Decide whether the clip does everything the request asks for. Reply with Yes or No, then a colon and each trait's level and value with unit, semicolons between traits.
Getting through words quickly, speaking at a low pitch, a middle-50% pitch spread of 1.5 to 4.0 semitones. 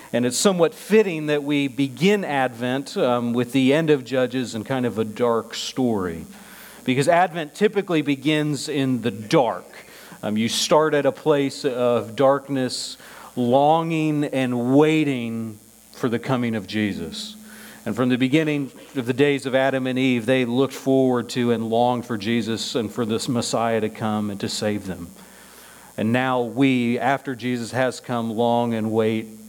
No: average, 165 wpm; low, 130 Hz; average, 3.3 semitones